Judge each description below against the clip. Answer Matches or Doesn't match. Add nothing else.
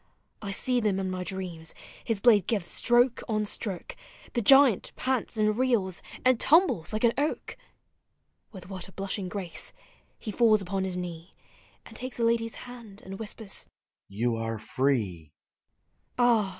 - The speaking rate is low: Doesn't match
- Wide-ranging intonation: Doesn't match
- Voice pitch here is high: Matches